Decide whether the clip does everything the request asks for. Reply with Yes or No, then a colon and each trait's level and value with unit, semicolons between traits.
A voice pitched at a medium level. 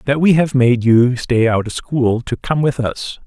No: low, 130 Hz